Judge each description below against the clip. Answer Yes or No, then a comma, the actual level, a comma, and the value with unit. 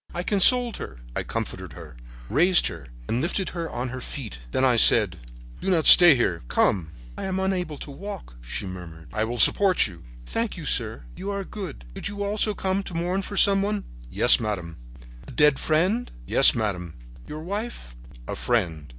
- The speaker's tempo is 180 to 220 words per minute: Yes, average, 185 wpm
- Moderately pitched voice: Yes, medium, 150 Hz